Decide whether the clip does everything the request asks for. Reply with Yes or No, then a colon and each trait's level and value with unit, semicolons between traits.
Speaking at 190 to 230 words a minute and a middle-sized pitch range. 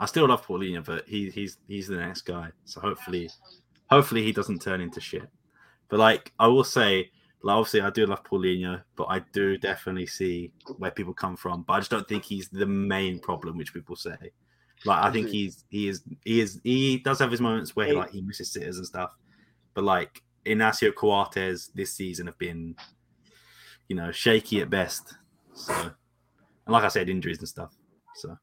Yes: average, 200 wpm; average, 3.1 semitones